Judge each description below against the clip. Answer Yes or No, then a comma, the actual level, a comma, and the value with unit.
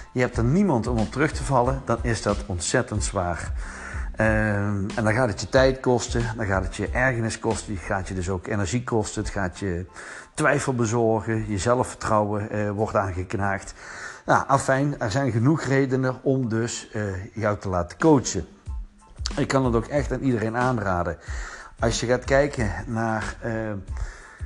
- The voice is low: Yes, low, 110 Hz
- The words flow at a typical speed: Yes, average, 175 wpm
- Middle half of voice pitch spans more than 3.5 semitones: Yes, average, 4.2 semitones